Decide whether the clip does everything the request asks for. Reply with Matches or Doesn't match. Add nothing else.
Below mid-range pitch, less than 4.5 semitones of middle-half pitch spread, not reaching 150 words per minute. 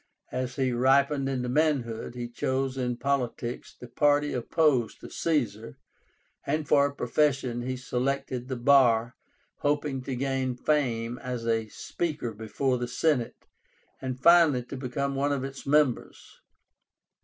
Matches